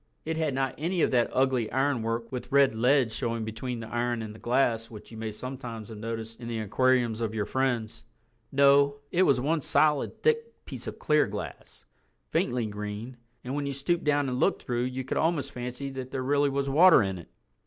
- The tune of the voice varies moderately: Yes, average, 3.6 semitones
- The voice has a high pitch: No, low, 125 Hz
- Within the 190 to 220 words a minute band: Yes, fast, 205 wpm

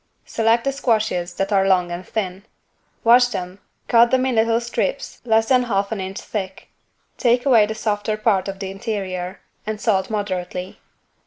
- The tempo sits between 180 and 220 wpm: No, average, 170 wpm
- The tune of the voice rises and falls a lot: No, average, 3.3 semitones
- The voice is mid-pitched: No, high, 210 Hz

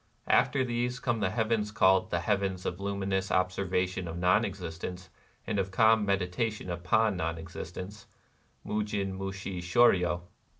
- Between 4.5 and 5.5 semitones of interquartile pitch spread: No, average, 2.7 semitones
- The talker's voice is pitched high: No, very low, 95 Hz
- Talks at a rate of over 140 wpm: No, slow, 135 wpm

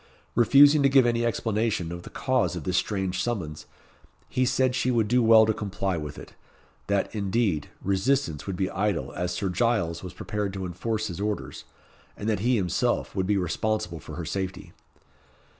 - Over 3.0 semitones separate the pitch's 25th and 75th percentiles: Yes, average, 4.4 semitones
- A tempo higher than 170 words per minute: Yes, average, 180 wpm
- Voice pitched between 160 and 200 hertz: No, low, 100 Hz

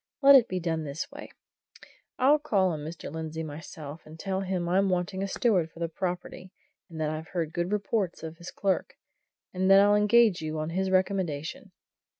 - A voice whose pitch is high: No, medium, 180 Hz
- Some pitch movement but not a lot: Yes, average, 3.4 semitones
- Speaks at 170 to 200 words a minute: Yes, average, 190 wpm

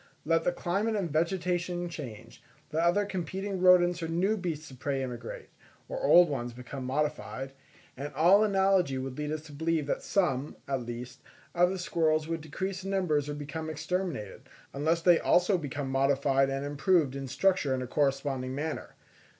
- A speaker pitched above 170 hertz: No, medium, 155 Hz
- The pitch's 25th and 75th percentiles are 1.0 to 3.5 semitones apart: No, average, 4.6 semitones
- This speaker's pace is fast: No, average, 175 wpm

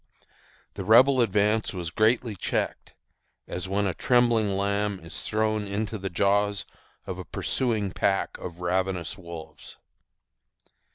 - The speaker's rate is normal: No, slow, 125 wpm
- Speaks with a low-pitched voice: Yes, low, 100 Hz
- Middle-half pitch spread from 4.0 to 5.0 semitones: No, narrow, 2.5 semitones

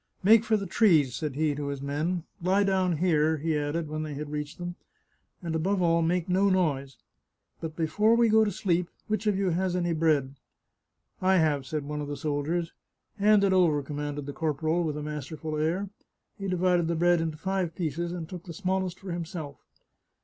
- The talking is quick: Yes, fast, 220 wpm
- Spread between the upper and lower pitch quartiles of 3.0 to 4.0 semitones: Yes, average, 3.6 semitones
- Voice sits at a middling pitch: Yes, medium, 165 Hz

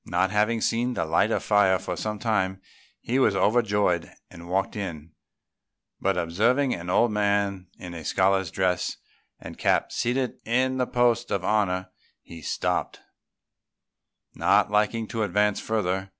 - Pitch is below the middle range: Yes, low, 100 Hz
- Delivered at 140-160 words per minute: Yes, average, 150 wpm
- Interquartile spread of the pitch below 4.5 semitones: Yes, average, 3.6 semitones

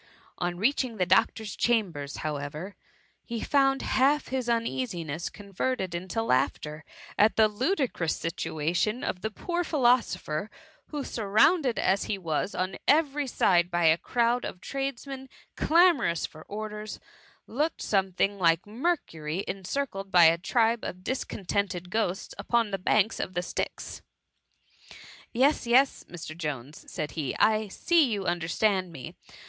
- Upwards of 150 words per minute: No, average, 140 wpm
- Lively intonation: Yes, wide, 6.2 semitones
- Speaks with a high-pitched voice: Yes, high, 205 Hz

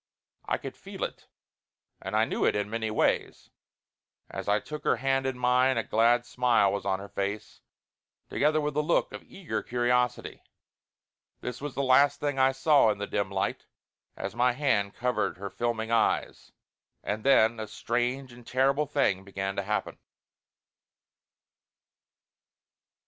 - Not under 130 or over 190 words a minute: Yes, average, 155 wpm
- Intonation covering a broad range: No, average, 4.4 semitones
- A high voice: No, low, 120 Hz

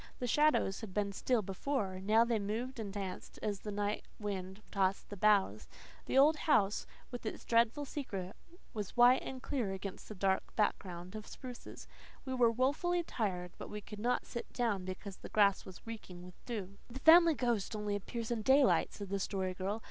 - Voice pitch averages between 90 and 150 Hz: No, high, 210 Hz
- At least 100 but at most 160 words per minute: No, average, 190 wpm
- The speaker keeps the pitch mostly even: No, average, 4.0 semitones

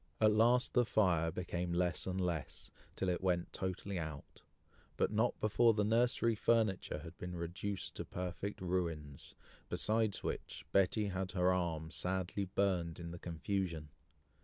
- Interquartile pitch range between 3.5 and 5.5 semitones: No, average, 3.1 semitones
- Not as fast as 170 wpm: Yes, average, 150 wpm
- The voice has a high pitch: No, very low, 90 Hz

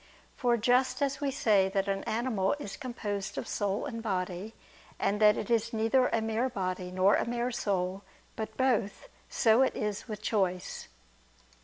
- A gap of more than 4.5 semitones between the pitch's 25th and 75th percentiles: No, average, 3.6 semitones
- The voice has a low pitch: No, high, 220 Hz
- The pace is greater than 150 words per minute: Yes, average, 170 wpm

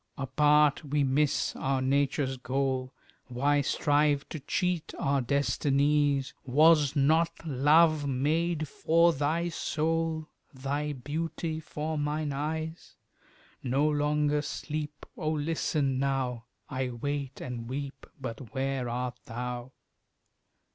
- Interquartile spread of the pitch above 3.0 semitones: No, narrow, 2.5 semitones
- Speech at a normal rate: No, slow, 115 wpm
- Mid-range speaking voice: Yes, medium, 145 Hz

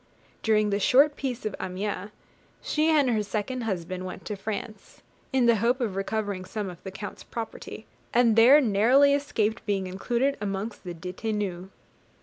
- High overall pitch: Yes, high, 215 Hz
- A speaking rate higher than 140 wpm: Yes, average, 160 wpm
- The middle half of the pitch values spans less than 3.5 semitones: No, average, 3.9 semitones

